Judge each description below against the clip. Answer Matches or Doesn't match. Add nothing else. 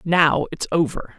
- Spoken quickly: Doesn't match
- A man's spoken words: Doesn't match